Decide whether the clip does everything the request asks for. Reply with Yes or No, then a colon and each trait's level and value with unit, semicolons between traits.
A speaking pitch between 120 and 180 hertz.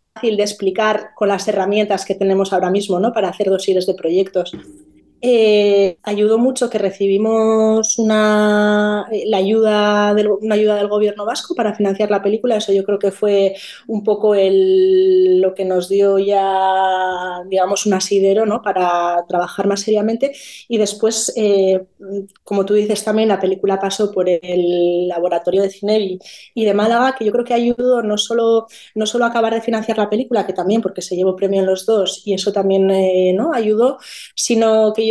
No: high, 205 Hz